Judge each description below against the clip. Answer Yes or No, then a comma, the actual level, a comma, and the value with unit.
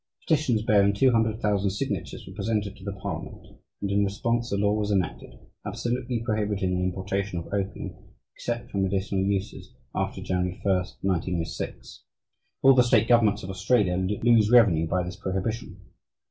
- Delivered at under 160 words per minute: Yes, average, 150 wpm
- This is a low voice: Yes, low, 100 Hz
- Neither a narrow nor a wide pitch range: Yes, average, 3.0 semitones